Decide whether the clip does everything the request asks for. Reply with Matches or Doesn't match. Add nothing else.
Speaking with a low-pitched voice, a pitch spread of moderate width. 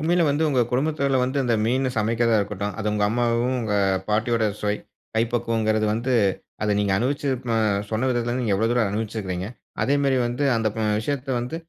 Matches